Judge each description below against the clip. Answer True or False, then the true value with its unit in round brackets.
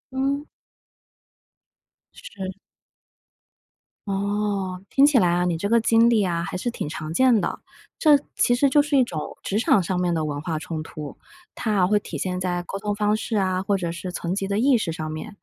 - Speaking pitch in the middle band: False (195 Hz)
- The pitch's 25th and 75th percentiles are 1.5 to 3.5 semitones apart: False (4.6 semitones)